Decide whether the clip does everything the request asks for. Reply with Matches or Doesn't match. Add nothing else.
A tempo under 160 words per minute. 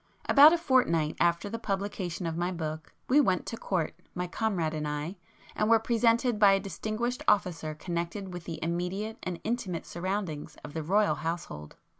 Doesn't match